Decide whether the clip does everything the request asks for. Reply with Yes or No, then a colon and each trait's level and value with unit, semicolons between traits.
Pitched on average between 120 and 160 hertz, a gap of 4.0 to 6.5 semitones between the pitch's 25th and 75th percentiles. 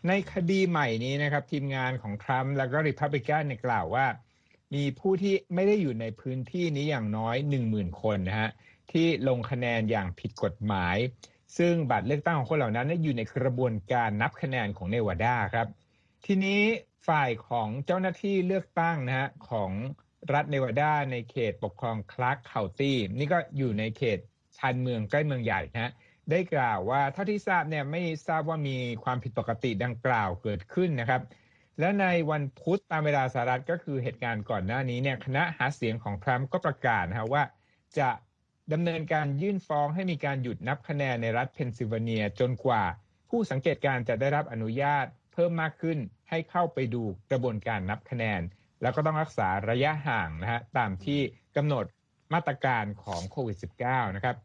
Yes: low, 130 Hz; average, 5.2 semitones